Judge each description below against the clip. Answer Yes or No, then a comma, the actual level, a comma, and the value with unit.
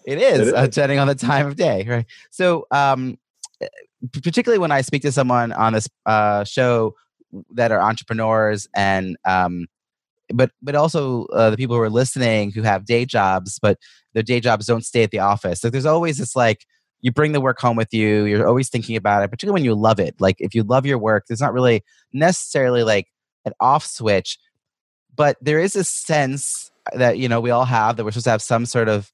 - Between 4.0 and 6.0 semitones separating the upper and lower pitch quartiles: Yes, average, 4.3 semitones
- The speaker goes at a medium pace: No, fast, 215 wpm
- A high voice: No, low, 120 Hz